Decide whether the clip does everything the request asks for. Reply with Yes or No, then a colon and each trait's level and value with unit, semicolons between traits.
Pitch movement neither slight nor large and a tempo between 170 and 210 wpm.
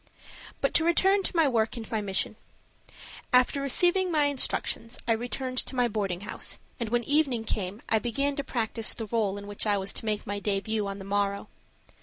Yes: average, 4.9 semitones; average, 200 wpm